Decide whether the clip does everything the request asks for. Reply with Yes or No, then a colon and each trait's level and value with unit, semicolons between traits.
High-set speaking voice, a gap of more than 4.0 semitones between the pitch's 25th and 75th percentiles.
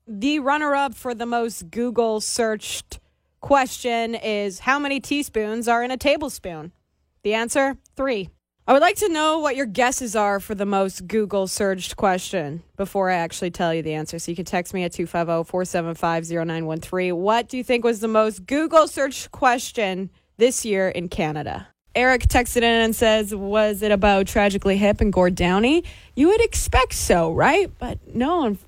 Yes: high, 215 Hz; wide, 5.4 semitones